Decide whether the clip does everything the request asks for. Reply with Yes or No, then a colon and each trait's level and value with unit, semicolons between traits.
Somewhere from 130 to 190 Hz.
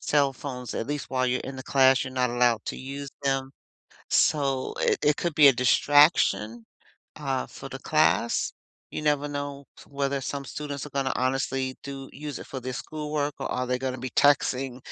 Yes: low, 135 Hz